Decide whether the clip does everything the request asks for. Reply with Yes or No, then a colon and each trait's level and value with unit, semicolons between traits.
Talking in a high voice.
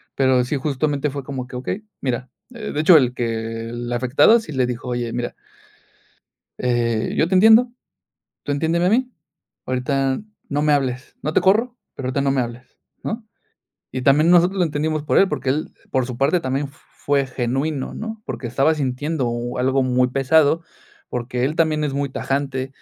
No: low, 135 Hz